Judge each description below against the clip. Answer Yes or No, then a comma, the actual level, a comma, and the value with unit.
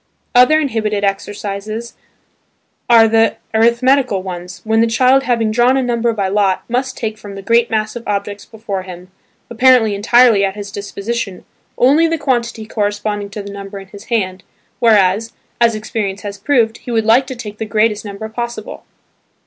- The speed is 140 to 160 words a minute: No, average, 170 wpm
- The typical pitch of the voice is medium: No, high, 220 Hz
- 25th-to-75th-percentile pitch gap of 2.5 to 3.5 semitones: Yes, average, 2.8 semitones